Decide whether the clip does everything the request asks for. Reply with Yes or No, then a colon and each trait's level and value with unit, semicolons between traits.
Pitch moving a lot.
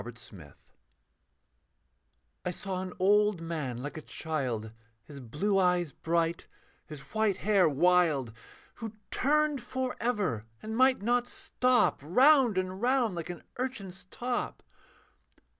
Yes: wide, 7.5 semitones